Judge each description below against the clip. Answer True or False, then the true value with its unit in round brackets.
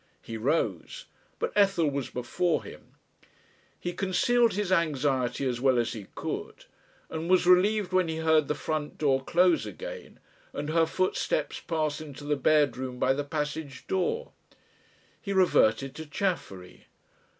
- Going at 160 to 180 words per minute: False (145 wpm)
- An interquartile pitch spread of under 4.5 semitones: False (5.1 semitones)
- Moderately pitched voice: True (155 Hz)